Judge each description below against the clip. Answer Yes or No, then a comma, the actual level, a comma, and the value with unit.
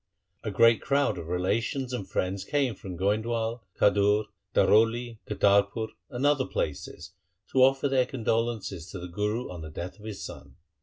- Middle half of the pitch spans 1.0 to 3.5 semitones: No, average, 3.9 semitones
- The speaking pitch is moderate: No, low, 110 Hz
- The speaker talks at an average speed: Yes, average, 160 wpm